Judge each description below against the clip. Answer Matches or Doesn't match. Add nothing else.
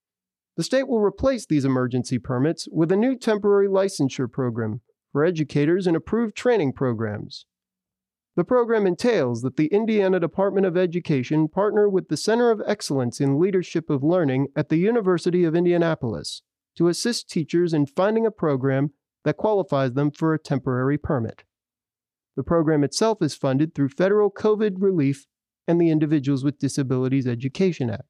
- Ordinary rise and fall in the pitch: Doesn't match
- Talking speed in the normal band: Matches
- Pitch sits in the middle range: Matches